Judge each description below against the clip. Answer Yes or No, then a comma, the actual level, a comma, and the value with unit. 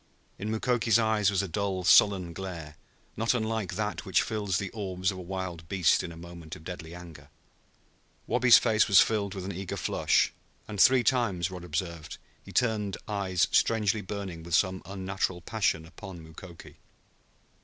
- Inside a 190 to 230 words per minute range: No, average, 165 wpm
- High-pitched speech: No, very low, 95 Hz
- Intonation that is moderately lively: Yes, average, 3.3 semitones